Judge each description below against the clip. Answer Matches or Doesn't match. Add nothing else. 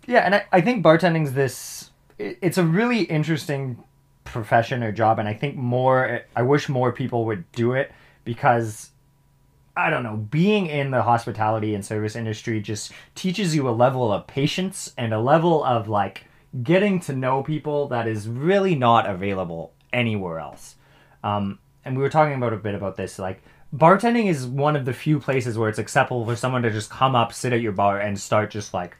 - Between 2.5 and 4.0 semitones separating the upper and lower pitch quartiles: Doesn't match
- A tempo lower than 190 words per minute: Doesn't match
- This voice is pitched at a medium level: Doesn't match